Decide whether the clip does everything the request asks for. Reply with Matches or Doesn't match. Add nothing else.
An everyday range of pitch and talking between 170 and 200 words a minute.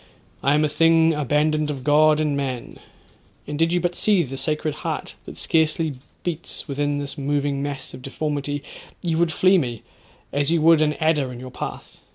Doesn't match